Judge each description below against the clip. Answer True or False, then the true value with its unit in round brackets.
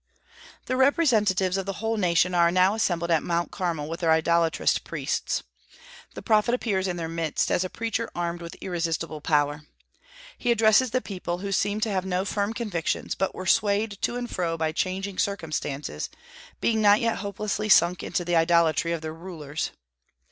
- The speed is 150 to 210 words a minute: True (175 wpm)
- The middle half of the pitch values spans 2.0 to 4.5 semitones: True (3.8 semitones)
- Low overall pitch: False (185 Hz)